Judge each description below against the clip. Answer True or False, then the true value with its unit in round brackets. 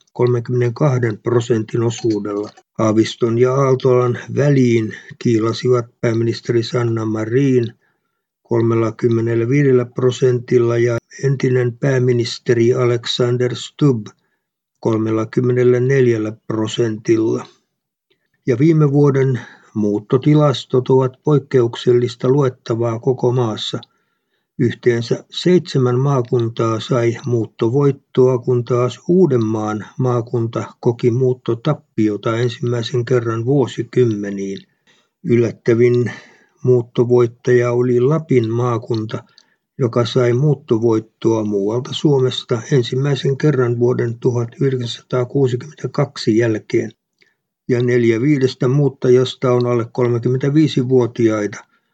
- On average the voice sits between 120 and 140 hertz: True (125 Hz)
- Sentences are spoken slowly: True (75 wpm)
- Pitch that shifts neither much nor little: False (2.0 semitones)